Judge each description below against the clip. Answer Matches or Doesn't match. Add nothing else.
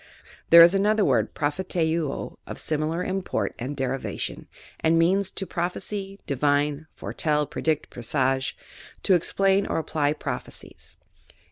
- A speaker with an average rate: Doesn't match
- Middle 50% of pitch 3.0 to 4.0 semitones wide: Doesn't match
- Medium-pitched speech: Matches